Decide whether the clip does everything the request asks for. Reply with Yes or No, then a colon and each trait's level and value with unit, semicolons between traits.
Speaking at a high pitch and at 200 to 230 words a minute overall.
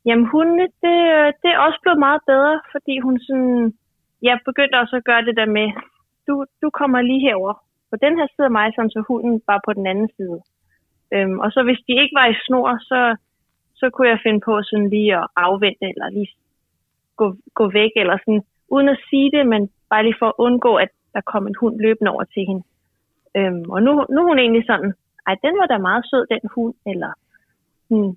Yes: high, 235 Hz; average, 215 wpm